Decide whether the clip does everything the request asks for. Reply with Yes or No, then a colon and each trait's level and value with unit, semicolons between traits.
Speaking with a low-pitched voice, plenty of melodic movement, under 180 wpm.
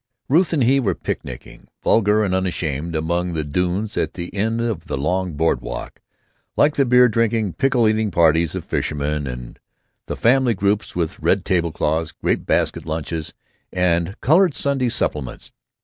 Yes: very low, 95 Hz; wide, 6.2 semitones; average, 165 wpm